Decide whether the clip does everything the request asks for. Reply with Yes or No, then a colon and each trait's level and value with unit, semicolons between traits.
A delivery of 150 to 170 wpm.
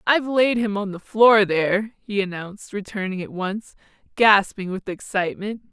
Yes: average, 155 wpm